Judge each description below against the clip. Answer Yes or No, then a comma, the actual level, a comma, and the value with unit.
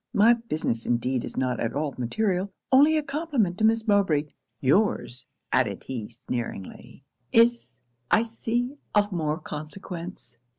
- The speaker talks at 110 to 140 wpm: Yes, slow, 135 wpm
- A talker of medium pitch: Yes, medium, 180 Hz